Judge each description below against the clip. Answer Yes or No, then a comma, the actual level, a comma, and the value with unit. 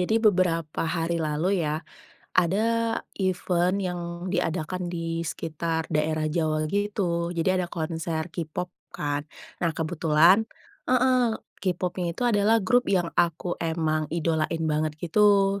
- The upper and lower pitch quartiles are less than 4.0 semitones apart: Yes, average, 3.2 semitones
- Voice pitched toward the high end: No, medium, 170 Hz